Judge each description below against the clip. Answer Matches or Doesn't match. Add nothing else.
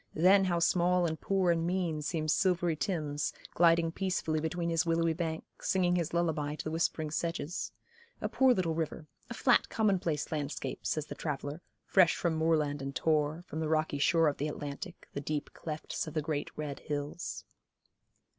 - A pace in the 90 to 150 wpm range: Doesn't match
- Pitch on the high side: Doesn't match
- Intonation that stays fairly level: Matches